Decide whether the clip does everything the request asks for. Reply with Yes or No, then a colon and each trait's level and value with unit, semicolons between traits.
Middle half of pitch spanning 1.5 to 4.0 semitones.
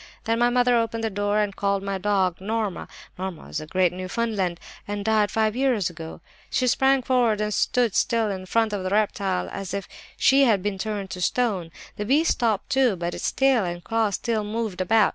Yes: average, 3.4 semitones